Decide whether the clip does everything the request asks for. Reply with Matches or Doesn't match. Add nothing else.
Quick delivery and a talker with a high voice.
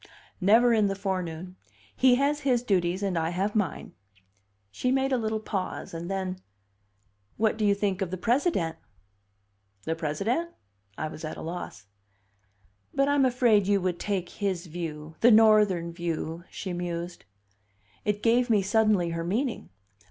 Doesn't match